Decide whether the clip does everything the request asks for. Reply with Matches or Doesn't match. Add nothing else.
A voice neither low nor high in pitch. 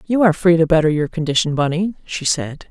Matches